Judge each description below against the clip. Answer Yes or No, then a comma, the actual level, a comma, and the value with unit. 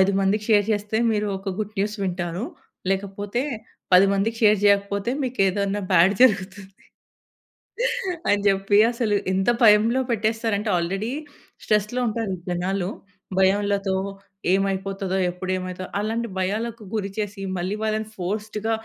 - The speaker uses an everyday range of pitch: No, narrow, 1.9 semitones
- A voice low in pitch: No, high, 200 Hz